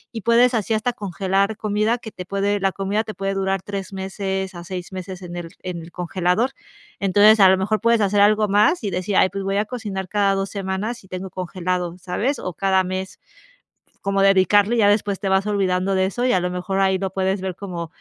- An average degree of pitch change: No, narrow, 1.8 semitones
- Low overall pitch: No, high, 195 Hz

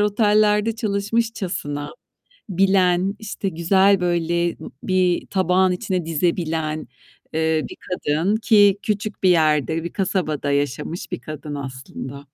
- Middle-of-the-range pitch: Yes, medium, 180 Hz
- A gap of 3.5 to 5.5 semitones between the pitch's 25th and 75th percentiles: Yes, average, 4.1 semitones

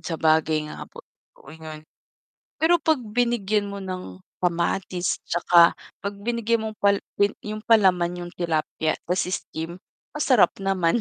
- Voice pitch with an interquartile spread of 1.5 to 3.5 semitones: No, average, 4.1 semitones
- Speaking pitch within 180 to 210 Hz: Yes, medium, 185 Hz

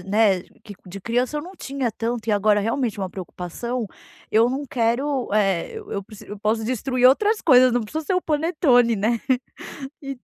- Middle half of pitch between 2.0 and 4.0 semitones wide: No, average, 4.5 semitones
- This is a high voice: Yes, high, 235 Hz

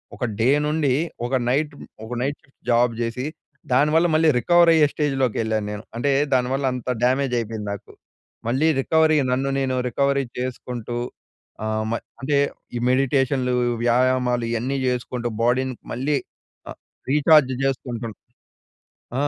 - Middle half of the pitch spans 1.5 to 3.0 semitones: Yes, narrow, 2.6 semitones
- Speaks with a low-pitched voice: Yes, low, 130 Hz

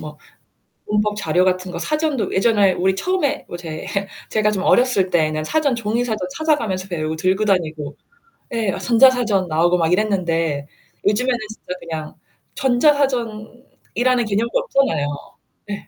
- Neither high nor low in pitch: No, high, 210 Hz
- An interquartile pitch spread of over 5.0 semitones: Yes, wide, 5.4 semitones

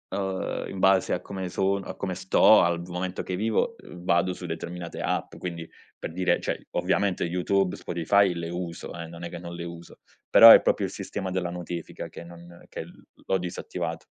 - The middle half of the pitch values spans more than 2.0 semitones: No, narrow, 1.7 semitones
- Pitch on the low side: Yes, very low, 90 Hz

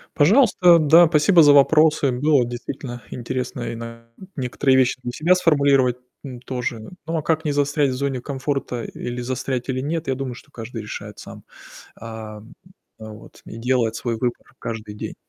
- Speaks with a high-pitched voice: No, low, 130 Hz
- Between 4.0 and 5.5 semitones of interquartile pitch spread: No, average, 3.4 semitones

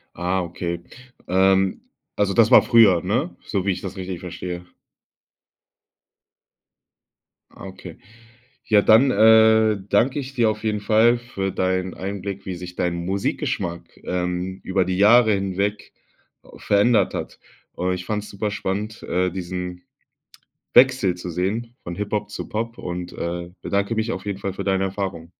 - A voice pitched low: Yes, very low, 95 Hz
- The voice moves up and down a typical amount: Yes, average, 3.0 semitones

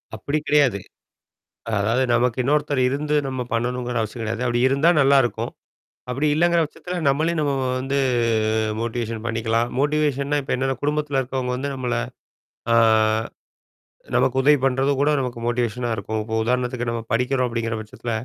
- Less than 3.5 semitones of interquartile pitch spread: Yes, average, 3.1 semitones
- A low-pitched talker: Yes, low, 125 Hz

